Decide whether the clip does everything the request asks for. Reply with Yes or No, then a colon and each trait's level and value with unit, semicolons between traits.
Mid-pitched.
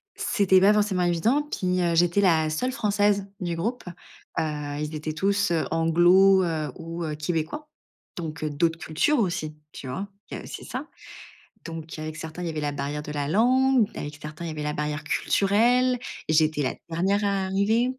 Yes: medium, 170 Hz